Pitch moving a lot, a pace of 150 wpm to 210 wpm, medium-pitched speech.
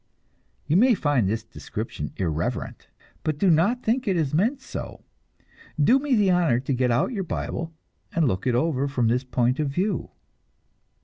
Yes: wide, 7.7 semitones; average, 175 wpm; medium, 155 Hz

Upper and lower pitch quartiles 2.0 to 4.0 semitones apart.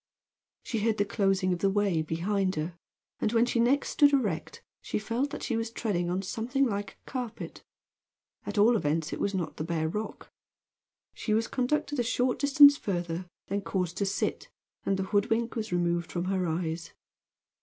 No: average, 4.8 semitones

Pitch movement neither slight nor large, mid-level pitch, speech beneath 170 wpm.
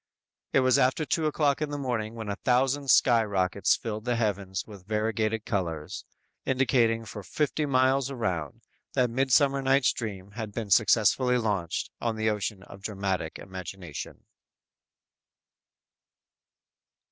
No: average, 4.5 semitones; low, 110 Hz; slow, 135 wpm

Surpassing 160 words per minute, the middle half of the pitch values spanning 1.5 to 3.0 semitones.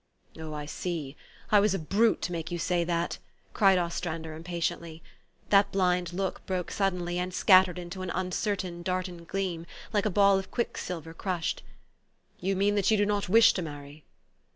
Yes: average, 180 wpm; narrow, 2.5 semitones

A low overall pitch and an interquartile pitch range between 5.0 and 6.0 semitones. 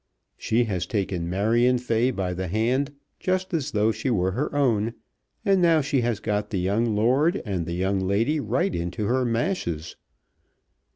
Yes: low, 115 Hz; wide, 5.5 semitones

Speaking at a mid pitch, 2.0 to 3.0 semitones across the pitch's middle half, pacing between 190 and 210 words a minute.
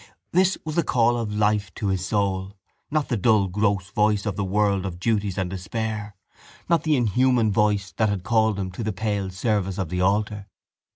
No: low, 105 Hz; narrow, 2.4 semitones; average, 195 wpm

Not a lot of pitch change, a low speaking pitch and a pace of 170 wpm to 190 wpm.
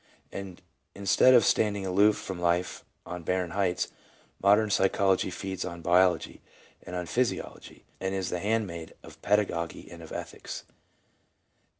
No: narrow, 2.3 semitones; very low, 95 Hz; average, 140 wpm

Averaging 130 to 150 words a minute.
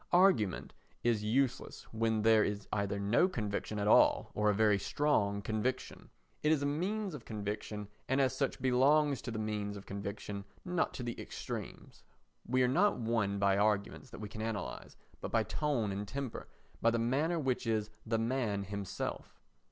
No: average, 175 wpm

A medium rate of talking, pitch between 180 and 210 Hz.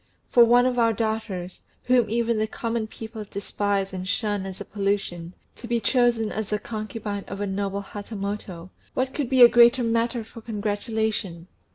No: average, 175 wpm; high, 220 Hz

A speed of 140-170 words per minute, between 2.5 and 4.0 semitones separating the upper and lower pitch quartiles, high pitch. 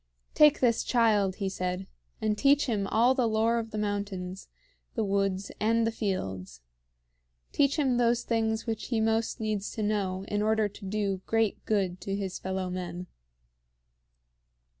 Yes: average, 160 wpm; average, 2.8 semitones; high, 210 Hz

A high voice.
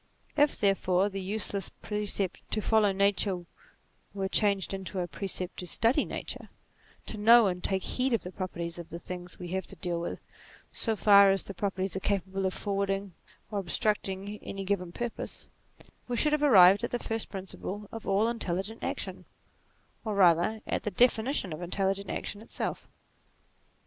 Yes: high, 195 Hz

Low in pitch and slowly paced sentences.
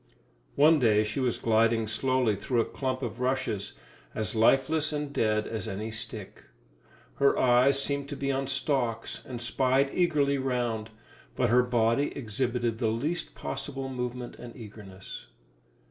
No: low, 125 Hz; average, 145 wpm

